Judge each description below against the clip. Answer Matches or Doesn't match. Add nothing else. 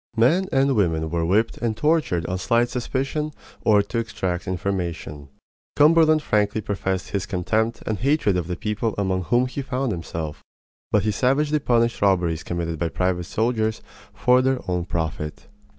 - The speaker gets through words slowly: Doesn't match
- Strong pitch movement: Matches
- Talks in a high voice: Doesn't match